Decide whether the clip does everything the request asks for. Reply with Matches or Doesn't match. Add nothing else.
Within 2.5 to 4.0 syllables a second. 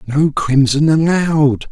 Matches